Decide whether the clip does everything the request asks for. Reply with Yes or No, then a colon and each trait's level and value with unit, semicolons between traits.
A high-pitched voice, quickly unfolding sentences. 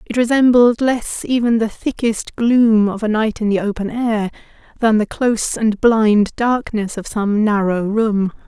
No: high, 220 Hz; average, 170 wpm